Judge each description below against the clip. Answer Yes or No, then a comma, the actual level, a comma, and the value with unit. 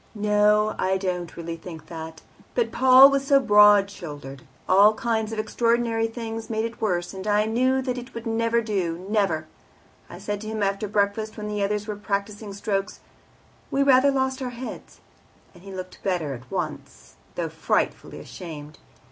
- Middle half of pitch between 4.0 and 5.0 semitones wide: No, average, 3.4 semitones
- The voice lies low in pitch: No, high, 210 Hz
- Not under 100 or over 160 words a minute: No, average, 175 wpm